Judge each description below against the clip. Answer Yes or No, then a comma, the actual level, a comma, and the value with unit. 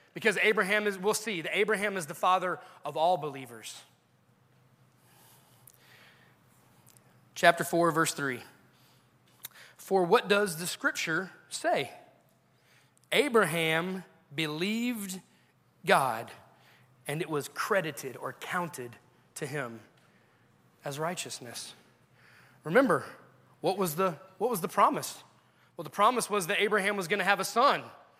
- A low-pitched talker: No, medium, 180 Hz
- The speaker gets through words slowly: Yes, slow, 120 wpm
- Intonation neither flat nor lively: No, wide, 5.9 semitones